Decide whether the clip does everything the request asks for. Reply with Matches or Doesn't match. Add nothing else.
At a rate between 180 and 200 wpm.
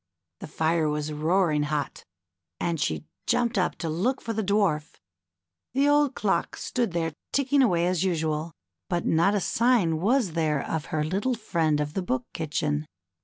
Doesn't match